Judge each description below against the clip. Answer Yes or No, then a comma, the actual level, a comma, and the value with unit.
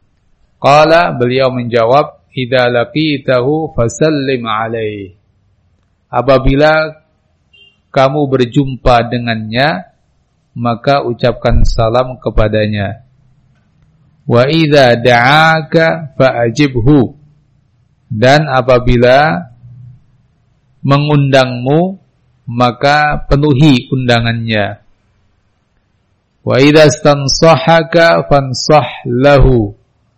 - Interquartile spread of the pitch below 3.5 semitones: No, average, 3.9 semitones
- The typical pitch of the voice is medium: No, low, 125 Hz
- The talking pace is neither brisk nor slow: No, slow, 60 wpm